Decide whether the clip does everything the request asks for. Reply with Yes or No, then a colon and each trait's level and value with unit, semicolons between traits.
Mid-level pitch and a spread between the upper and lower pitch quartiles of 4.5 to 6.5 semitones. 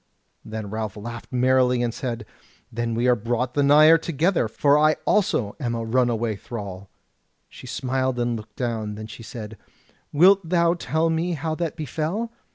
No: low, 125 Hz; wide, 5.6 semitones